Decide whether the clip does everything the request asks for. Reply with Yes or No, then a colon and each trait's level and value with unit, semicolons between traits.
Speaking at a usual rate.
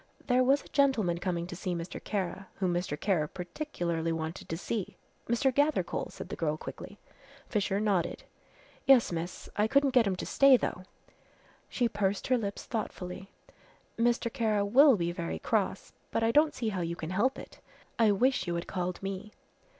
Yes: average, 180 wpm